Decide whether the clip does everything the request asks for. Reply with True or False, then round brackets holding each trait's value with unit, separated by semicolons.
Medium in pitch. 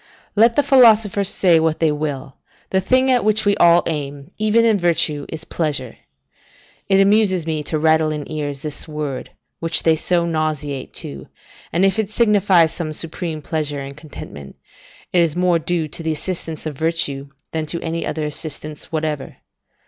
True (160 Hz)